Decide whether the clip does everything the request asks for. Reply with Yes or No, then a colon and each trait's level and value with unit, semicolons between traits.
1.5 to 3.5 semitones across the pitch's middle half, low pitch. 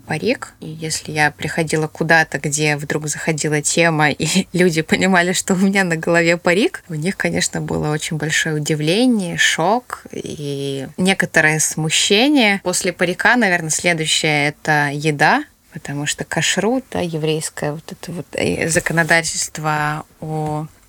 No: average, 2.8 semitones; medium, 160 Hz